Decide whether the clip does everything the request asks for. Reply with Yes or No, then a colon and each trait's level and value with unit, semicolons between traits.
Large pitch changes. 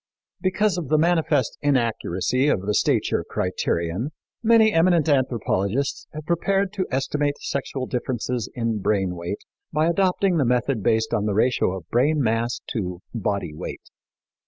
Yes: wide, 6.7 semitones